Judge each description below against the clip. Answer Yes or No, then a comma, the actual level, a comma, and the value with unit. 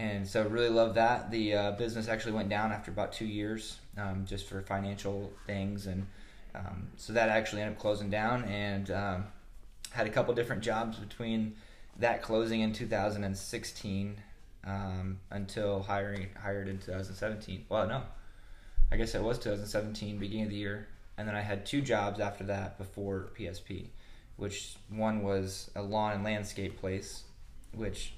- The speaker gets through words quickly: No, average, 165 wpm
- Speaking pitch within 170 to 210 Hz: No, low, 100 Hz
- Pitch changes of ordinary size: No, narrow, 1.8 semitones